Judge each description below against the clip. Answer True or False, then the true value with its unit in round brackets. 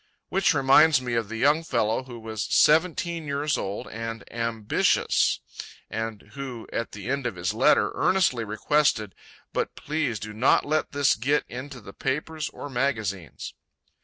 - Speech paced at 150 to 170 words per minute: True (155 wpm)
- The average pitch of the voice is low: True (125 Hz)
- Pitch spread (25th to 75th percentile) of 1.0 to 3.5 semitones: False (4.7 semitones)